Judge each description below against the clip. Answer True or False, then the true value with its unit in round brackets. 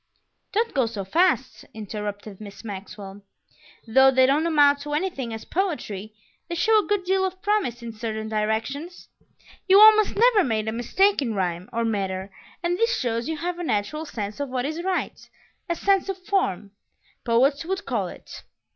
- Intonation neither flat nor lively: False (8.9 semitones)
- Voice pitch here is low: False (265 Hz)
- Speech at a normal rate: True (175 wpm)